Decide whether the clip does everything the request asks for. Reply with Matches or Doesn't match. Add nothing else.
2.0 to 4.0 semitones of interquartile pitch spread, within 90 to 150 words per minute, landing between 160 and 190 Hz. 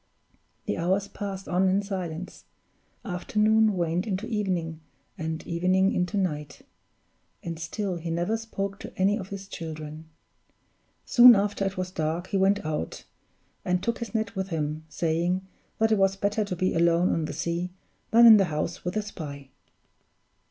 Doesn't match